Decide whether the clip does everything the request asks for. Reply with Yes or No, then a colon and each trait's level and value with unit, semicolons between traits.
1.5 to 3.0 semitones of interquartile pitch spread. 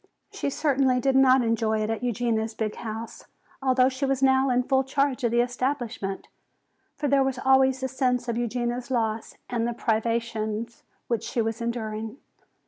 Yes: narrow, 2.6 semitones